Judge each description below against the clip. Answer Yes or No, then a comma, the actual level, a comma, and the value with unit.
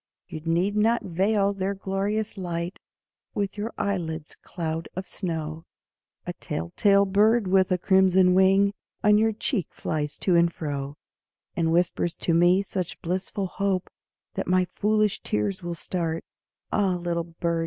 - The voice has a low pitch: No, medium, 185 Hz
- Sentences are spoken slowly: No, average, 150 wpm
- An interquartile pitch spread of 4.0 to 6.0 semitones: No, average, 2.9 semitones